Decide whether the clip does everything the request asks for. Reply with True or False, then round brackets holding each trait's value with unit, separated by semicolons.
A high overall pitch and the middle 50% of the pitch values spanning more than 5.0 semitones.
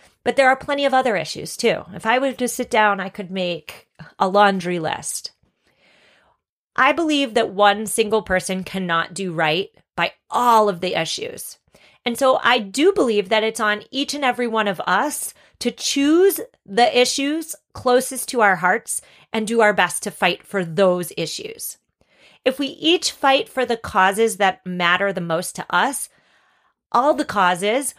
True (225 Hz; 5.5 semitones)